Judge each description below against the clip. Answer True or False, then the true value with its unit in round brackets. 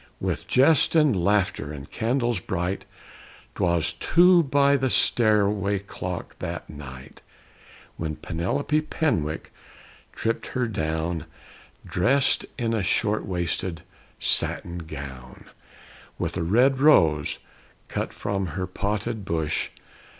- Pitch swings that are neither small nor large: False (6.7 semitones)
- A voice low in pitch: True (95 Hz)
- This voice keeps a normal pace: False (115 wpm)